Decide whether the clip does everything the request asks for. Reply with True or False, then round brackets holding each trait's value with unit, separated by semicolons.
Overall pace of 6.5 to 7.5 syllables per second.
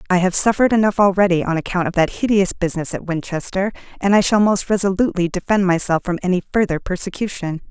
True (6.6 syllables/s)